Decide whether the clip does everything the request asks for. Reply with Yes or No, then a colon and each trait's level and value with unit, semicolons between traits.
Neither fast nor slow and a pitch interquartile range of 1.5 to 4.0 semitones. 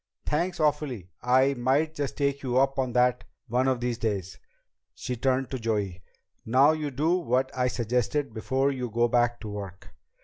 Yes: average, 175 wpm; average, 2.9 semitones